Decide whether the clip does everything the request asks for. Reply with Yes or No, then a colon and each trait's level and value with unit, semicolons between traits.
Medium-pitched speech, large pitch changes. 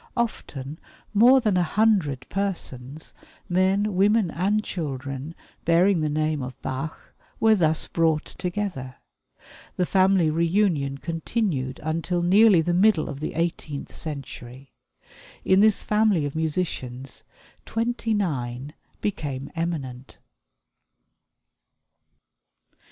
Yes: medium, 165 Hz; wide, 5.8 semitones